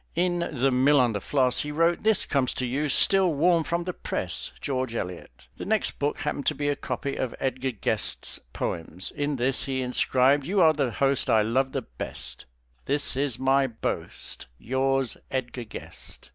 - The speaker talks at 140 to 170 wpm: No, average, 185 wpm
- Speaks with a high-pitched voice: No, low, 135 Hz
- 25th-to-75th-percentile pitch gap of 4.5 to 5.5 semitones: No, average, 2.8 semitones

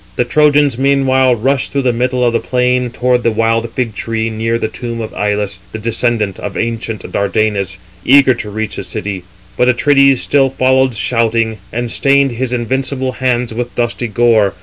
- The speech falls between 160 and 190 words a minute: Yes, average, 175 wpm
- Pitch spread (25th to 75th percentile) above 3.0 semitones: No, average, 2.7 semitones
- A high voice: No, low, 120 Hz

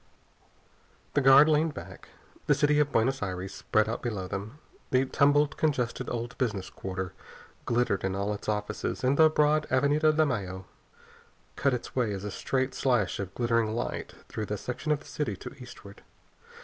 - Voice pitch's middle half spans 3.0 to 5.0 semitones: No, wide, 5.6 semitones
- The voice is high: No, low, 120 Hz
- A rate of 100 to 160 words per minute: No, average, 175 wpm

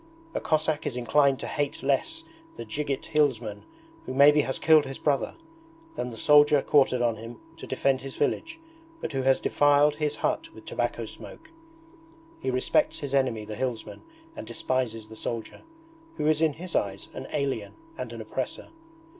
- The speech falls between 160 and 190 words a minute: Yes, average, 170 wpm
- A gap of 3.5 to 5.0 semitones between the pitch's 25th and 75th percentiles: No, average, 3.1 semitones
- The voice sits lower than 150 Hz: Yes, medium, 140 Hz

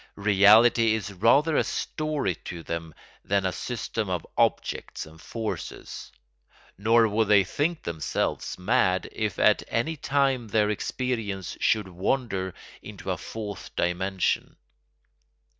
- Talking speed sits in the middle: No, slow, 125 wpm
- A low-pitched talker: Yes, low, 105 Hz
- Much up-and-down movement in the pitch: No, average, 3.9 semitones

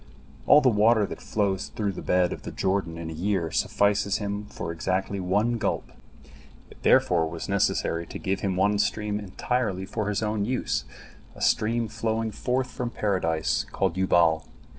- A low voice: Yes, low, 100 Hz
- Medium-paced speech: Yes, average, 170 wpm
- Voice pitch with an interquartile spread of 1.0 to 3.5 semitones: Yes, average, 3.0 semitones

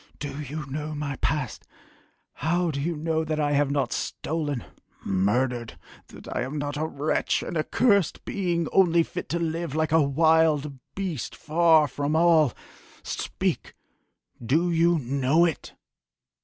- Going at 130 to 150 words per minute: Yes, average, 145 wpm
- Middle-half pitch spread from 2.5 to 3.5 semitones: Yes, average, 2.8 semitones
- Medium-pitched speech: Yes, medium, 155 Hz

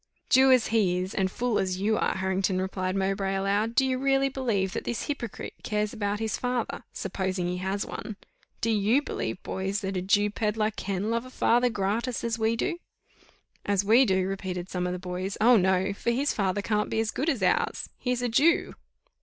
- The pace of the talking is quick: Yes, fast, 210 wpm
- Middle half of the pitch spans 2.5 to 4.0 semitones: Yes, average, 3.7 semitones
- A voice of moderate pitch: No, high, 205 Hz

